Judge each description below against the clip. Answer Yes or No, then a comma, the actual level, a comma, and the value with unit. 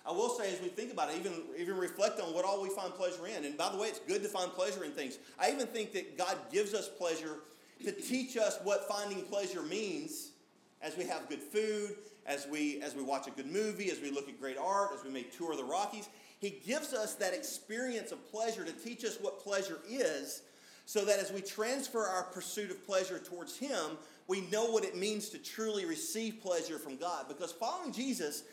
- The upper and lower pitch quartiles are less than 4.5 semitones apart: No, average, 5.3 semitones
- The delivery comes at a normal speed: No, fast, 225 wpm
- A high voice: Yes, high, 205 Hz